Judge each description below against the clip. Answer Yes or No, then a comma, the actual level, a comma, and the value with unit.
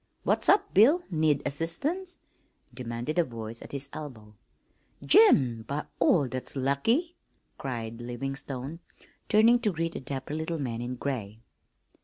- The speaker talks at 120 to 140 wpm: Yes, slow, 135 wpm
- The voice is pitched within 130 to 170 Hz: Yes, medium, 140 Hz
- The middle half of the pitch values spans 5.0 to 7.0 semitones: Yes, wide, 5.5 semitones